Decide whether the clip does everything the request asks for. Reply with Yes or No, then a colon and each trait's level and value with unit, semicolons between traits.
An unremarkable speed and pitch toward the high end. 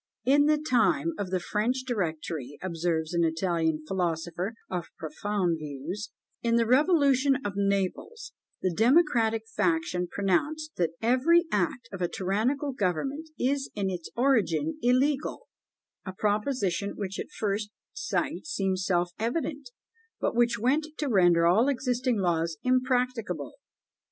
No: slow, 130 wpm; high, 210 Hz